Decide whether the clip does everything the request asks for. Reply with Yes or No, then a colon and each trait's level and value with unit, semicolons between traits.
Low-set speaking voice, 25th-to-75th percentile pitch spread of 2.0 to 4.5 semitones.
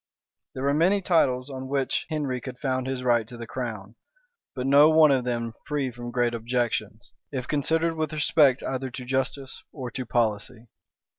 Yes: low, 130 Hz; average, 2.8 semitones